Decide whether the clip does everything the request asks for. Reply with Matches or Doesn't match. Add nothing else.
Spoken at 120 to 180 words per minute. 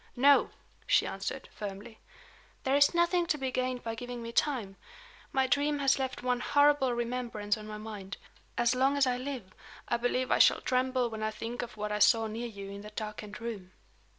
Doesn't match